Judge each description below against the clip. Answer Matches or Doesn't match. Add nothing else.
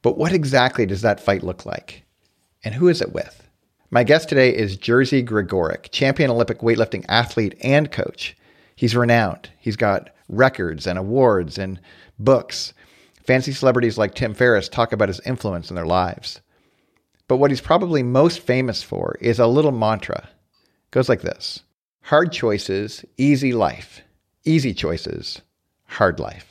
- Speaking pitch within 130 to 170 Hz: Doesn't match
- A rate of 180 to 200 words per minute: Doesn't match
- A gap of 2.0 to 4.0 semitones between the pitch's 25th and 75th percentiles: Doesn't match